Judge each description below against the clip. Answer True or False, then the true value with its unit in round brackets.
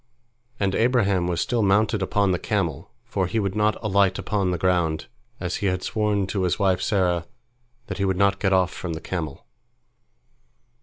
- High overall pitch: False (95 Hz)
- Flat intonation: True (2.3 semitones)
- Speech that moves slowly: False (185 wpm)